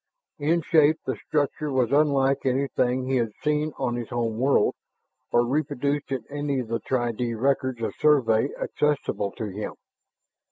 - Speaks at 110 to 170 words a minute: Yes, average, 160 wpm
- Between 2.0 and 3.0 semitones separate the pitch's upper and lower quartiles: No, average, 3.4 semitones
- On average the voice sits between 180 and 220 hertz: No, low, 130 Hz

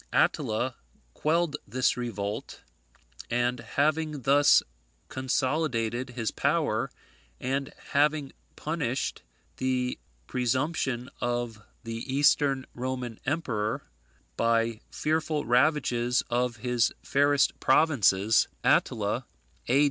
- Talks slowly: Yes, slow, 85 wpm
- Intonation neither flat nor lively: Yes, average, 3.4 semitones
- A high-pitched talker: No, low, 130 Hz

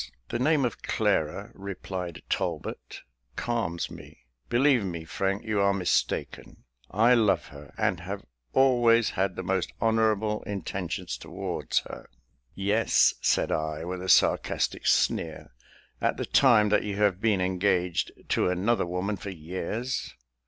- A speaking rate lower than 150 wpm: Yes, average, 140 wpm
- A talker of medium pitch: No, low, 100 Hz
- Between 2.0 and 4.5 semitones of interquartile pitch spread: Yes, average, 3.6 semitones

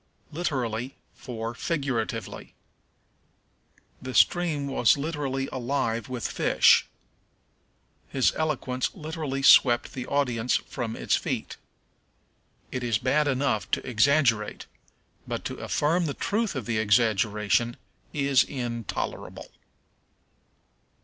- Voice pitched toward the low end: Yes, low, 130 Hz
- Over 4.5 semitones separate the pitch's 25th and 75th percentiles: No, average, 3.6 semitones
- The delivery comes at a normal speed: No, slow, 100 wpm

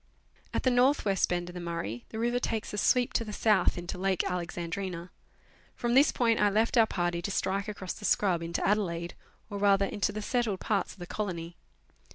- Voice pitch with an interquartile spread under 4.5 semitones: Yes, average, 4.0 semitones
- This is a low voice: No, high, 200 Hz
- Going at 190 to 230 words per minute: Yes, fast, 205 wpm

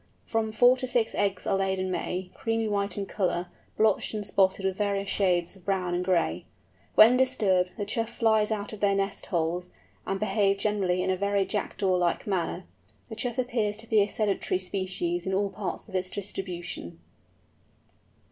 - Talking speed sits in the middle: Yes, average, 185 wpm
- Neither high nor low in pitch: No, high, 195 Hz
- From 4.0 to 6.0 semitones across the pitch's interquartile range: No, narrow, 2.5 semitones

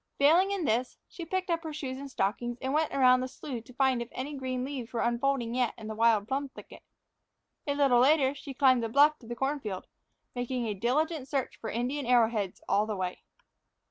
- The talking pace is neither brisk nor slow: No, fast, 220 wpm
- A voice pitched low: No, very high, 255 Hz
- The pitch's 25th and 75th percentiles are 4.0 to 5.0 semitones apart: No, average, 3.3 semitones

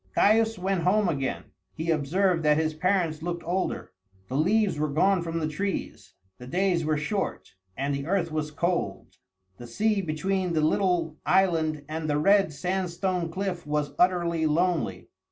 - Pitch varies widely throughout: No, average, 3.6 semitones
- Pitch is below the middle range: No, medium, 170 Hz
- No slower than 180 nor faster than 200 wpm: No, average, 160 wpm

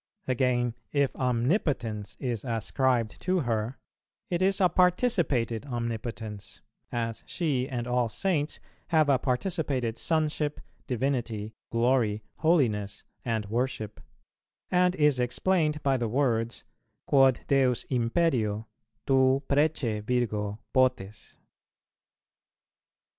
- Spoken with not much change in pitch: No, average, 4.3 semitones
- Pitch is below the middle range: Yes, low, 125 Hz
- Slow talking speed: Yes, slow, 100 wpm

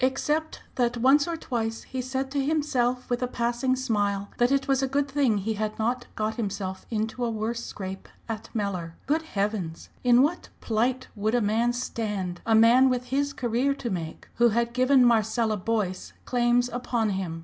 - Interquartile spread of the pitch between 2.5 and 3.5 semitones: Yes, average, 3.2 semitones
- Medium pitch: No, high, 235 Hz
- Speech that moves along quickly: No, average, 185 wpm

